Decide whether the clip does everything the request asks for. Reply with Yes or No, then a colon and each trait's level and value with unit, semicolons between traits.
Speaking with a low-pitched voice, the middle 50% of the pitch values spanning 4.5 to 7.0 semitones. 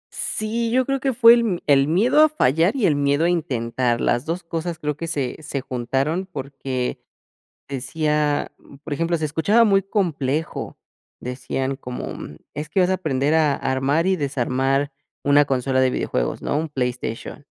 No: medium, 150 Hz; average, 4.8 semitones